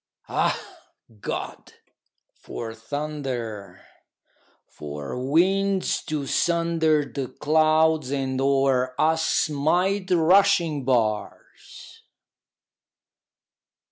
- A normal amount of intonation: Yes, average, 4.1 semitones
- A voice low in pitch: No, medium, 150 Hz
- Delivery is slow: Yes, slow, 70 wpm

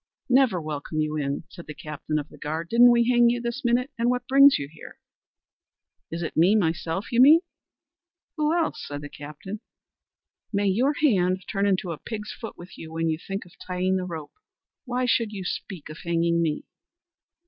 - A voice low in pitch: No, medium, 185 Hz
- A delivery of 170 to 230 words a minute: Yes, average, 190 wpm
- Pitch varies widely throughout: Yes, wide, 6.8 semitones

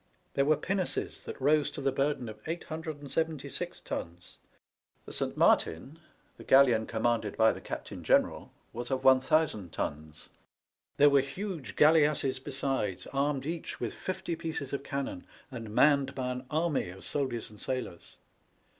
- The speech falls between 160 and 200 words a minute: No, average, 145 wpm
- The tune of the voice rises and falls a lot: No, average, 4.1 semitones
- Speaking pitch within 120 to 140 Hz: Yes, low, 135 Hz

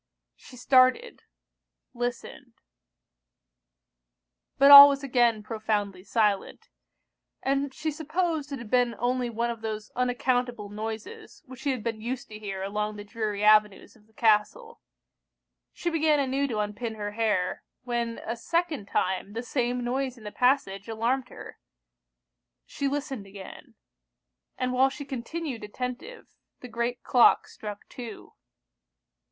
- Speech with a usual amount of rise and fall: Yes, average, 4.0 semitones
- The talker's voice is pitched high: Yes, high, 240 Hz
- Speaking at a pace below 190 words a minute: Yes, slow, 135 wpm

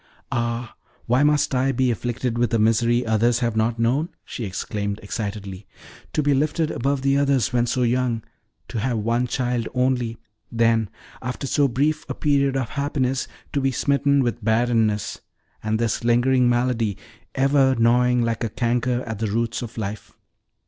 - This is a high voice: No, low, 120 Hz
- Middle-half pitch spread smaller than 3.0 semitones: Yes, narrow, 2.5 semitones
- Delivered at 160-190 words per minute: Yes, average, 165 wpm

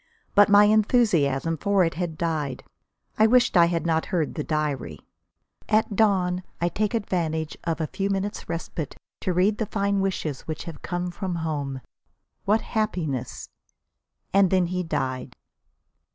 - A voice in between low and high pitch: Yes, medium, 175 Hz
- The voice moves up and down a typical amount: Yes, average, 4.1 semitones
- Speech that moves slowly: No, average, 155 wpm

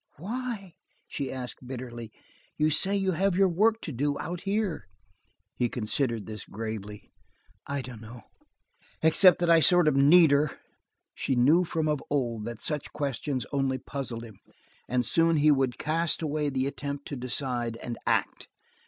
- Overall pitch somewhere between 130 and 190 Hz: Yes, medium, 140 Hz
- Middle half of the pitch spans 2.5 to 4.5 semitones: No, average, 5.2 semitones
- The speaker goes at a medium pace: Yes, average, 160 wpm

